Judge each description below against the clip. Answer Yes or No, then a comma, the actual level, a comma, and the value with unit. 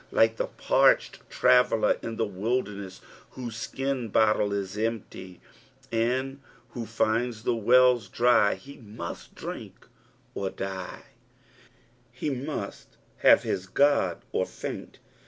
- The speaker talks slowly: Yes, slow, 120 wpm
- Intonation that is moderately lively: Yes, average, 3.7 semitones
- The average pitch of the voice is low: Yes, low, 115 Hz